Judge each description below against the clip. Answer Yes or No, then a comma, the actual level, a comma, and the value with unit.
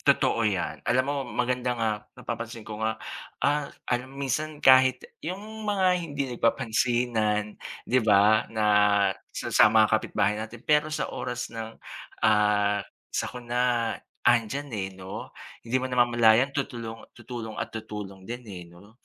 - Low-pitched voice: Yes, low, 115 Hz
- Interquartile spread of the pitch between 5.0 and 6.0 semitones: No, average, 3.0 semitones